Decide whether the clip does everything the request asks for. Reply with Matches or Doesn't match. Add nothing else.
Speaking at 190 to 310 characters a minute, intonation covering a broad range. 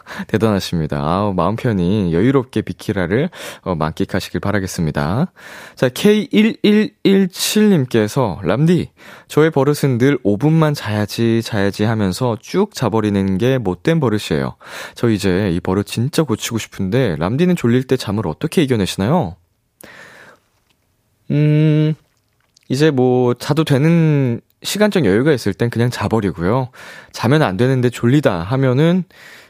Matches